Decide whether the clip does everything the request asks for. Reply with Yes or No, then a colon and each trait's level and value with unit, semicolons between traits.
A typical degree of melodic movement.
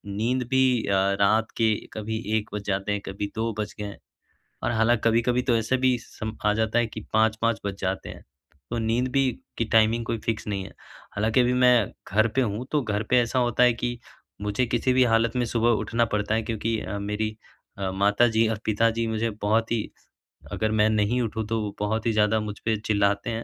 No: narrow, 2.0 semitones